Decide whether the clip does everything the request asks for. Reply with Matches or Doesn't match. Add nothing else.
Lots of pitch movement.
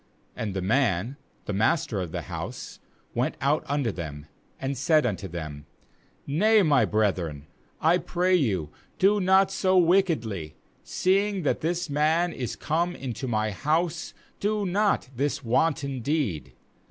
Matches